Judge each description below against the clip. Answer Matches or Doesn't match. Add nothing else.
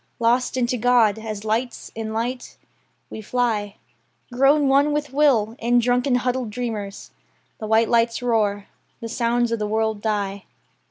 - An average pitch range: Doesn't match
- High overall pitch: Matches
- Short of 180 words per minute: Matches